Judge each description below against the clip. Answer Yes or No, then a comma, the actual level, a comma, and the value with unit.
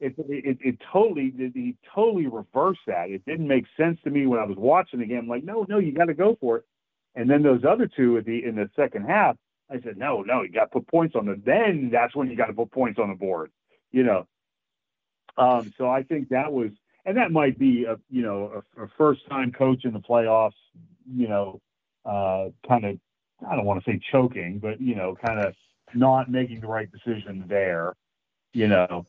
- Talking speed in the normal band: No, fast, 225 wpm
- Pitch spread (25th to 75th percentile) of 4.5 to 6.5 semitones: Yes, average, 4.8 semitones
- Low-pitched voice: Yes, low, 125 Hz